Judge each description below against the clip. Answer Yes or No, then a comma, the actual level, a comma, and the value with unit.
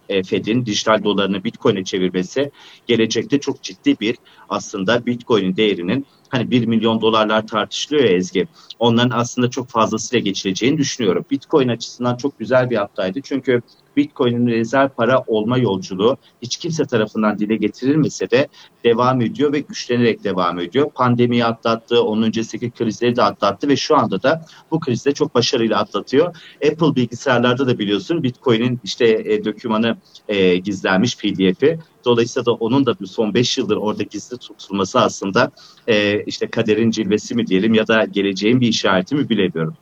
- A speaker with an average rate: No, fast, 150 wpm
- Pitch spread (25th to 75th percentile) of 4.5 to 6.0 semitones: No, average, 3.1 semitones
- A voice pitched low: Yes, low, 115 Hz